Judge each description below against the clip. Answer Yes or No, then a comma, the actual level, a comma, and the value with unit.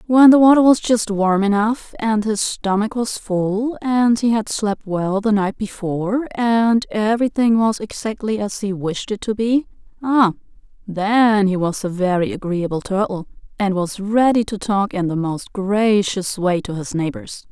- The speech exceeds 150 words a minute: Yes, average, 170 wpm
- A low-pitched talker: No, high, 210 Hz